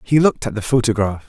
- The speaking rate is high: Yes, fast, 235 wpm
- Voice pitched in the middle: No, low, 115 Hz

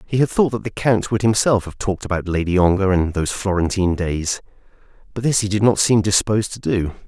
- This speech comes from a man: Yes, male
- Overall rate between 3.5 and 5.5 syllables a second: No, 6.1 syllables/s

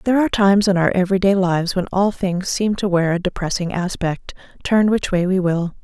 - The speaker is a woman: Yes, female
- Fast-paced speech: Yes, fast, 225 wpm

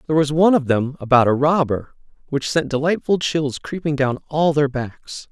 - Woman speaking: No, male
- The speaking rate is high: No, average, 190 wpm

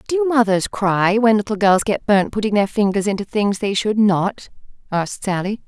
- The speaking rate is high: No, average, 190 wpm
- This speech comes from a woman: Yes, female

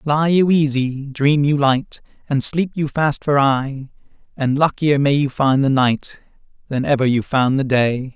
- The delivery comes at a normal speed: Yes, average, 185 wpm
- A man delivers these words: Yes, male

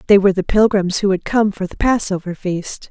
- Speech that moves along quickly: Yes, fast, 225 wpm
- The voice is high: Yes, high, 195 Hz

